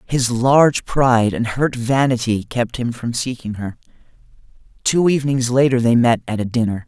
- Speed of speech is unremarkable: Yes, average, 165 wpm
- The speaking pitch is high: No, low, 120 Hz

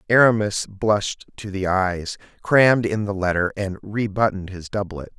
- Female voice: No, male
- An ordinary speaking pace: Yes, average, 160 wpm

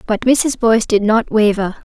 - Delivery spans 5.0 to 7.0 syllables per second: No, 4.8 syllables/s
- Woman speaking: Yes, female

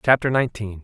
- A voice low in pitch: Yes, low, 115 Hz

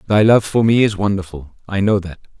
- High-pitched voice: No, low, 100 Hz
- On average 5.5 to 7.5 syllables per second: Yes, 5.7 syllables/s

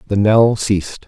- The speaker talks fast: No, average, 165 wpm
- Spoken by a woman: No, male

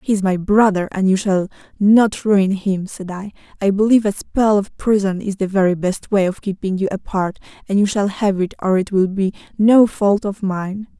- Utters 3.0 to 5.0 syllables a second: Yes, 4.8 syllables/s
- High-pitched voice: Yes, high, 200 Hz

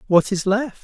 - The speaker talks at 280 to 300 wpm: No, fast, 215 wpm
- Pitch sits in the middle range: No, high, 205 Hz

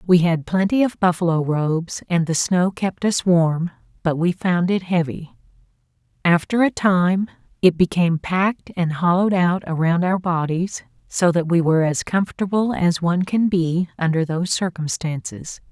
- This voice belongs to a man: No, female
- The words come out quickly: No, average, 160 wpm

